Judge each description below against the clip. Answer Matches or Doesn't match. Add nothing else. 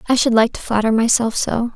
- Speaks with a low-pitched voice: Doesn't match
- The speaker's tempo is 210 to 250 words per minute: Matches